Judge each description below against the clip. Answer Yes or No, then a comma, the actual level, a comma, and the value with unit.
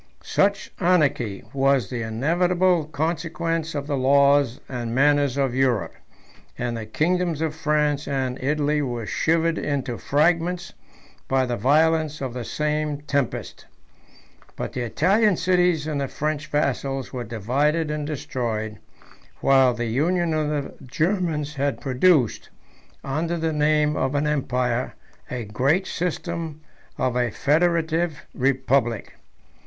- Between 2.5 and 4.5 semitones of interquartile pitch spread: Yes, average, 3.8 semitones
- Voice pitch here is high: No, medium, 145 Hz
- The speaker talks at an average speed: No, slow, 130 wpm